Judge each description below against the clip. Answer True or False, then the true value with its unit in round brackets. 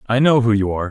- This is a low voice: True (115 Hz)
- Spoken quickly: True (330 wpm)